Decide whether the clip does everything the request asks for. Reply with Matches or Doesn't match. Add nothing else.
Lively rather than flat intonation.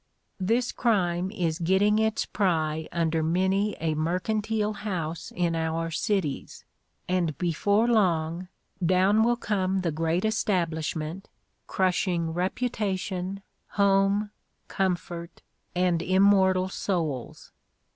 Doesn't match